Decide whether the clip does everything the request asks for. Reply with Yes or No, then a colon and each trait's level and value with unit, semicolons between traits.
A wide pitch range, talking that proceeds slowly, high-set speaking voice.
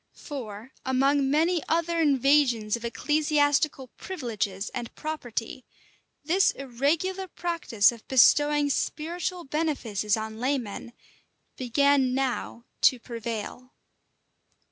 No: average, 4.5 semitones; slow, 95 wpm; very high, 270 Hz